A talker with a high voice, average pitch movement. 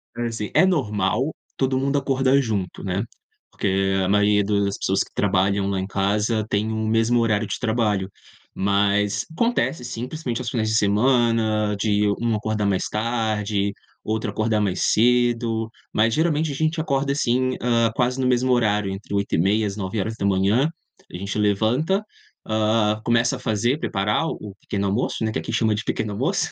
No: low, 110 Hz; average, 3.2 semitones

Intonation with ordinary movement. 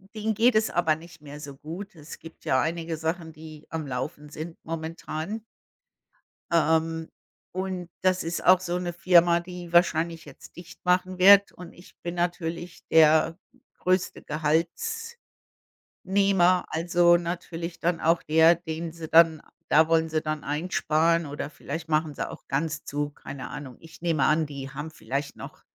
No: narrow, 2.0 semitones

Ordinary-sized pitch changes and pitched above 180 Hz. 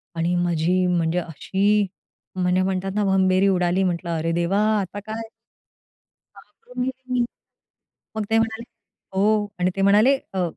Yes: average, 3.0 semitones; high, 190 Hz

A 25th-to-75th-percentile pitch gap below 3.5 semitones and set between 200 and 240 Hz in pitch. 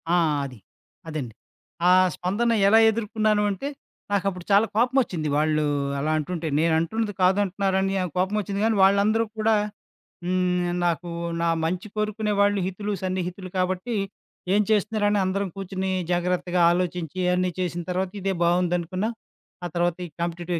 No: average, 2.8 semitones; medium, 185 Hz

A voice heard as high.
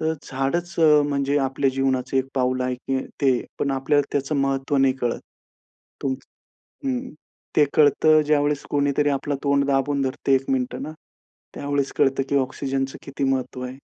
No: low, 135 Hz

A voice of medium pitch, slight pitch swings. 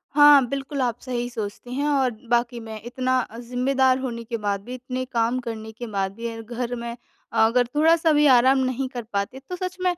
No: high, 245 Hz; narrow, 2.3 semitones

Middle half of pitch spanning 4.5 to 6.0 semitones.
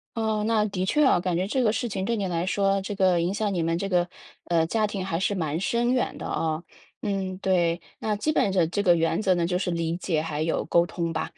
No: average, 3.4 semitones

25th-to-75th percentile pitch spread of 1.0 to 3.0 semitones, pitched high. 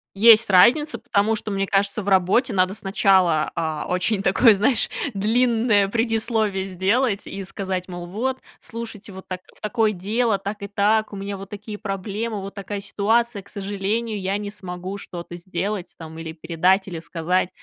Yes: average, 2.7 semitones; high, 200 Hz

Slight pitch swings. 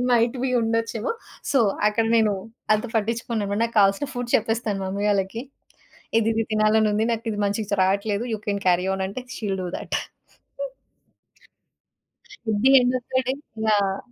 Yes: narrow, 2.3 semitones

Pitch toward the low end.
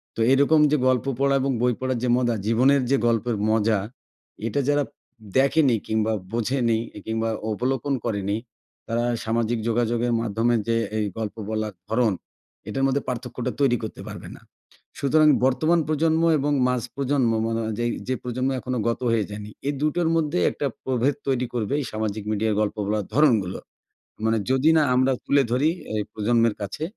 Yes: low, 120 Hz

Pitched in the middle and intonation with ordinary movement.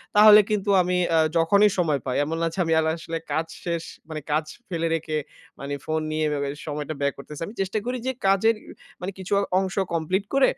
Yes: medium, 165 Hz; average, 3.9 semitones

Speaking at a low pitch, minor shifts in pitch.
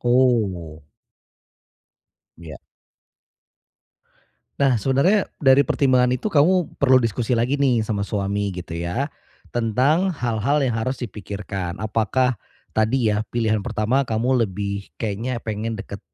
No: low, 115 Hz; average, 4.1 semitones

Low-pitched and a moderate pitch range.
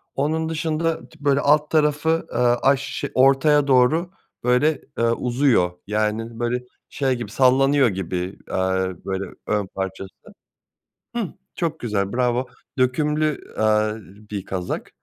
No: low, 130 Hz; wide, 5.7 semitones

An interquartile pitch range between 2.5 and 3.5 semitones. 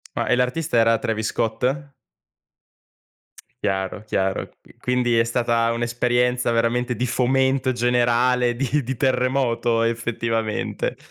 No: narrow, 1.6 semitones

